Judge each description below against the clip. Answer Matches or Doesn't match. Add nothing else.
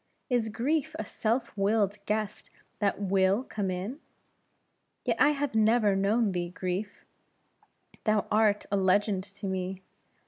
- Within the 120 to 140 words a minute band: Matches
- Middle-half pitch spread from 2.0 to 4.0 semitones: Matches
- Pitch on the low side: Doesn't match